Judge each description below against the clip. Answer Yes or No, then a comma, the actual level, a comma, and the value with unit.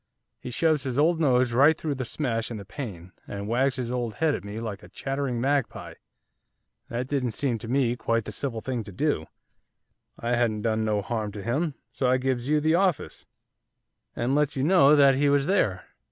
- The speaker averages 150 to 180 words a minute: No, fast, 205 wpm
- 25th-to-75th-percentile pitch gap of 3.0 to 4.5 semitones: Yes, average, 3.9 semitones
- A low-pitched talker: Yes, low, 125 Hz